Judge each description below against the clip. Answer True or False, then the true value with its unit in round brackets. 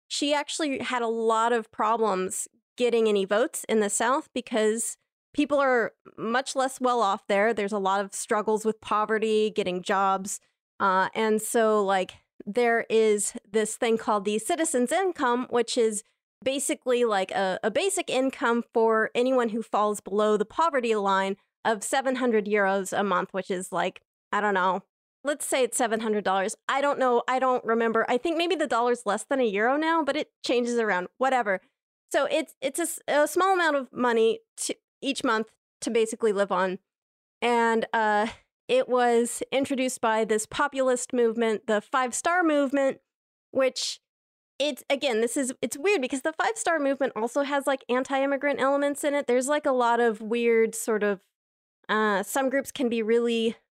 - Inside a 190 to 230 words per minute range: False (175 wpm)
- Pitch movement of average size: True (4.0 semitones)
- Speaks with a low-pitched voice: False (235 Hz)